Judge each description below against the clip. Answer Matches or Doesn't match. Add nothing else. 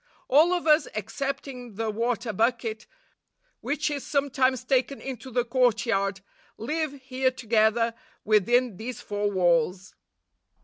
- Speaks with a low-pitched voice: Doesn't match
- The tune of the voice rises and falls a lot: Doesn't match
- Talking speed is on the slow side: Matches